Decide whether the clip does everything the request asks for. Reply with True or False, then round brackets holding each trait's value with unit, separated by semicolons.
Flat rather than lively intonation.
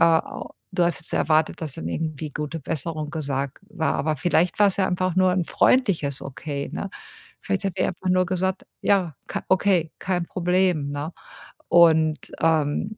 False (3.3 semitones)